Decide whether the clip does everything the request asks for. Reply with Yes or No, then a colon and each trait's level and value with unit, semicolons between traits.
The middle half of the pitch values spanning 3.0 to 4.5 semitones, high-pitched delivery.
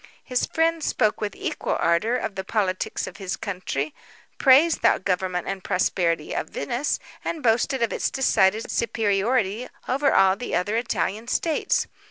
No: average, 5.0 semitones; high, 210 Hz